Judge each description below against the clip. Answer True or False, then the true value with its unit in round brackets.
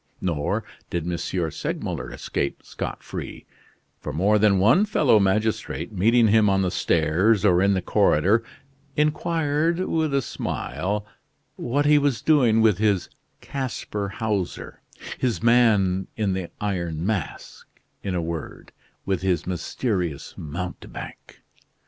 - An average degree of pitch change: True (4.5 semitones)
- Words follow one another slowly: True (130 wpm)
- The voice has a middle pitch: False (100 Hz)